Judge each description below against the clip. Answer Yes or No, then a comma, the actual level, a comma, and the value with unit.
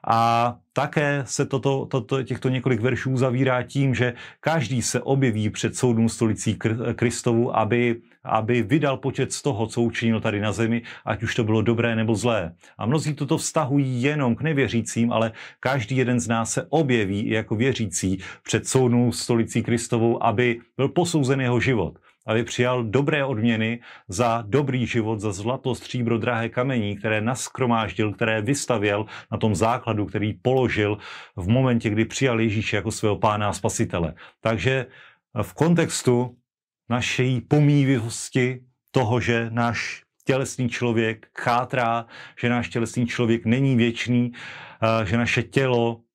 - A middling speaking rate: Yes, average, 150 wpm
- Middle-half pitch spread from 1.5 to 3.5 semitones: Yes, narrow, 2.4 semitones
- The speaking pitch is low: Yes, low, 120 Hz